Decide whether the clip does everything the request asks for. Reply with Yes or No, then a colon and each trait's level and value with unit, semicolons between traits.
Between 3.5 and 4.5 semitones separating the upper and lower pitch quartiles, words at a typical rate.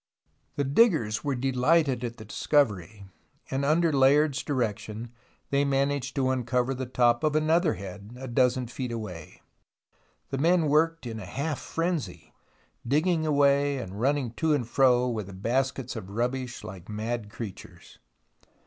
Yes: average, 3.8 semitones; average, 150 wpm